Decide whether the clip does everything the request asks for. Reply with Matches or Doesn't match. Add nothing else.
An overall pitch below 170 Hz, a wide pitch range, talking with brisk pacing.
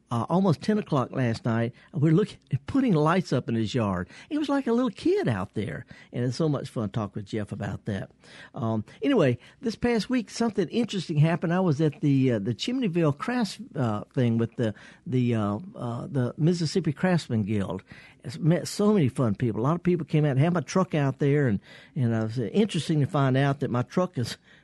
Matches